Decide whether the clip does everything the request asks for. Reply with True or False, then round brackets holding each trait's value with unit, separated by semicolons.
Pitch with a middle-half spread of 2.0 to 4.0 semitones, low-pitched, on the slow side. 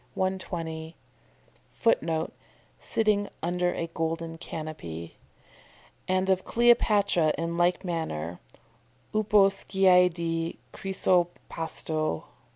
False (2.8 semitones; 170 Hz; 85 wpm)